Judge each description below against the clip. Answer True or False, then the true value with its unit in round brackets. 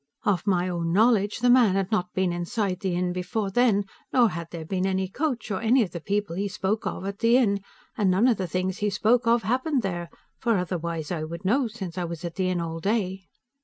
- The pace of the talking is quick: True (240 wpm)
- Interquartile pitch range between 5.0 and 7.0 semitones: False (3.9 semitones)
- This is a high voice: True (195 Hz)